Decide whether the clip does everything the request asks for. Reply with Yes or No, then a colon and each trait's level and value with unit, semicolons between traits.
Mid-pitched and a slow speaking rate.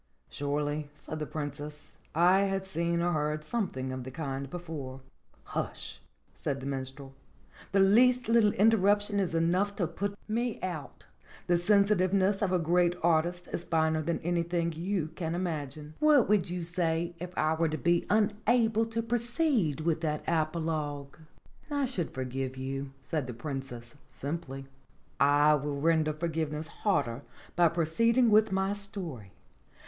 No: medium, 170 Hz; average, 155 wpm